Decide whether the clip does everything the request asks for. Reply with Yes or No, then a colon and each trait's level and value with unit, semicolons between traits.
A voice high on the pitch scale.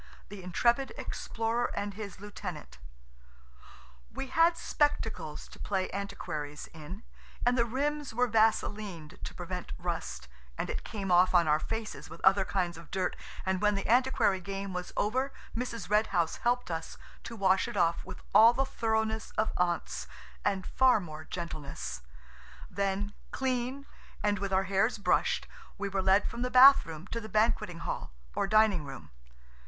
Yes: high, 200 Hz